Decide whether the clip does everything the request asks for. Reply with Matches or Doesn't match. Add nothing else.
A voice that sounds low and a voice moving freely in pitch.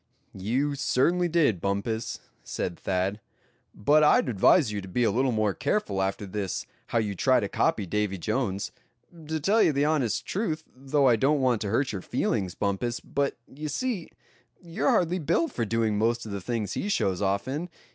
Matches